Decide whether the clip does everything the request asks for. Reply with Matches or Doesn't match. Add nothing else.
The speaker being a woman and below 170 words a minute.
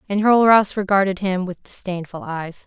Matches